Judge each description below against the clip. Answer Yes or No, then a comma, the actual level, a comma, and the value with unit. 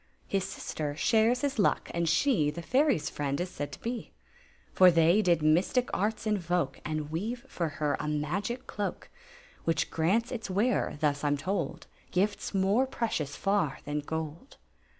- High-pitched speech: No, medium, 175 Hz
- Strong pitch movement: Yes, wide, 6.0 semitones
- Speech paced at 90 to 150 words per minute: No, average, 165 wpm